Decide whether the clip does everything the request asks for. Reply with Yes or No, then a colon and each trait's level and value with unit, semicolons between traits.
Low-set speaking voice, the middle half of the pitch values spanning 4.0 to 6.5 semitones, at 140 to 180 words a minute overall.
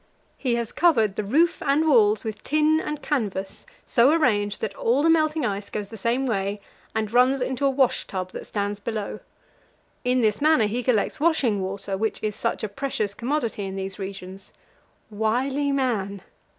No: high, 225 Hz; average, 5.2 semitones; average, 175 wpm